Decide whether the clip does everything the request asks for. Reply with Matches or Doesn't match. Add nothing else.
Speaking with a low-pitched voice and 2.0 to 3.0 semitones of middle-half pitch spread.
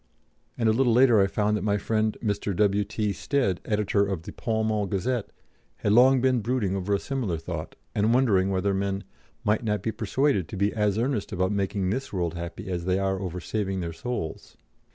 Matches